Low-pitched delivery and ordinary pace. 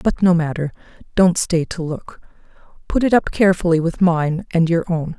No: medium, 170 Hz; average, 185 wpm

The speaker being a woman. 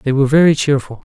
No: male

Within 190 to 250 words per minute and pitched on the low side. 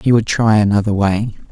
Yes: average, 200 wpm; low, 105 Hz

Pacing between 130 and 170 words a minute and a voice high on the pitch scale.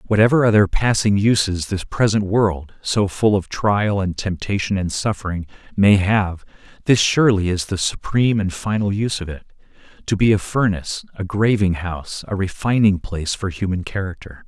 No: average, 160 wpm; low, 100 Hz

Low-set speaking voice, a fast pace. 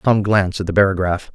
Yes: very low, 95 Hz; fast, 225 wpm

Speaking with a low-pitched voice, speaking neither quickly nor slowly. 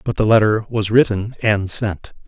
Yes: low, 105 Hz; average, 185 wpm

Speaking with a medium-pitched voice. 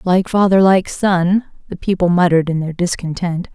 Yes: medium, 180 Hz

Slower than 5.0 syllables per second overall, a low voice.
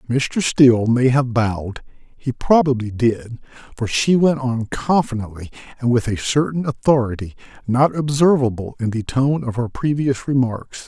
Yes: 4.5 syllables/s; low, 125 Hz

